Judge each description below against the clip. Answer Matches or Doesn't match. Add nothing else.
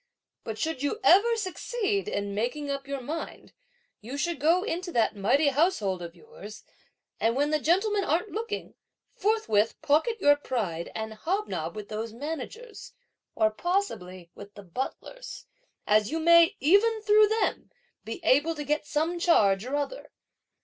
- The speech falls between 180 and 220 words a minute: Doesn't match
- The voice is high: Matches